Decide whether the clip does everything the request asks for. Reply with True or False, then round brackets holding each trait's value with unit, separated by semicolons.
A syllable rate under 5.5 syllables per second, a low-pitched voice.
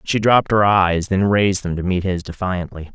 True (5.3 syllables/s; 95 Hz)